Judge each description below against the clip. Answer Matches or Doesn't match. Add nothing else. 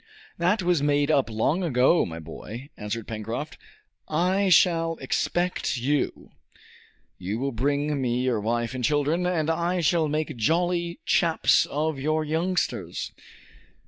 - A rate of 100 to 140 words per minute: Matches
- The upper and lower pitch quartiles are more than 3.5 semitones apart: Matches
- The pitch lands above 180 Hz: Doesn't match